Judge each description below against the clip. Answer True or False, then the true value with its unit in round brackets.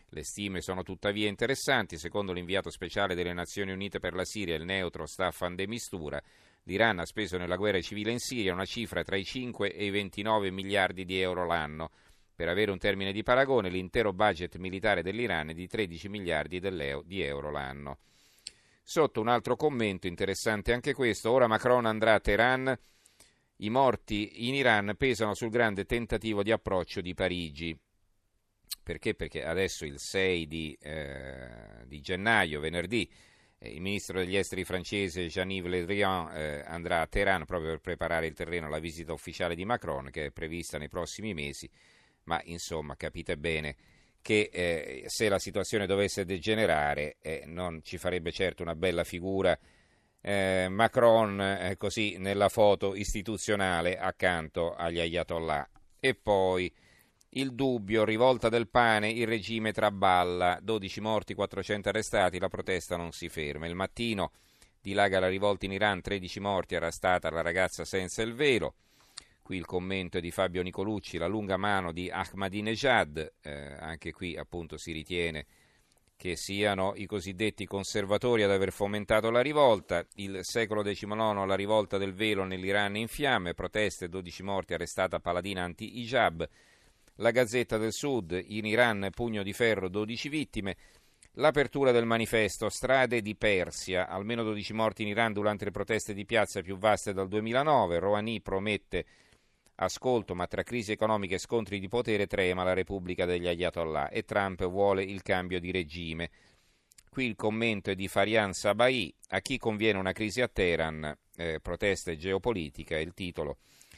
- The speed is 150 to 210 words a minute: True (155 wpm)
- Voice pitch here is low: True (95 Hz)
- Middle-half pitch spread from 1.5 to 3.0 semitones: False (3.4 semitones)